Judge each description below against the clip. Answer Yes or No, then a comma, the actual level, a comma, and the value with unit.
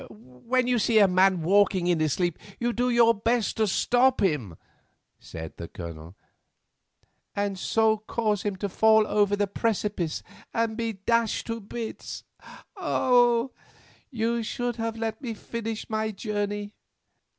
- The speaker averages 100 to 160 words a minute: Yes, average, 145 wpm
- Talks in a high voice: Yes, high, 215 Hz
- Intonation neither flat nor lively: Yes, average, 3.3 semitones